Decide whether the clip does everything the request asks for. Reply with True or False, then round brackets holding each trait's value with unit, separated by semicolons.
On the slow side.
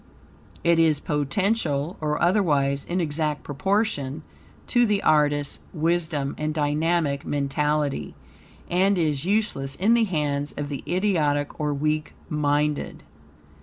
True (120 wpm)